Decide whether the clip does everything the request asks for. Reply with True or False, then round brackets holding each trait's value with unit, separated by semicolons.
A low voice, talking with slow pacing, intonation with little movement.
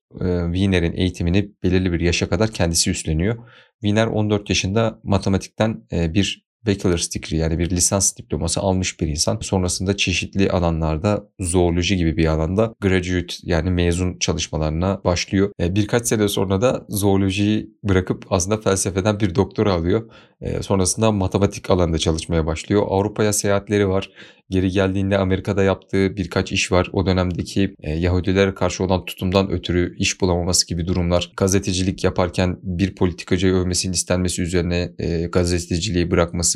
False (95 Hz; 130 wpm; 2.3 semitones)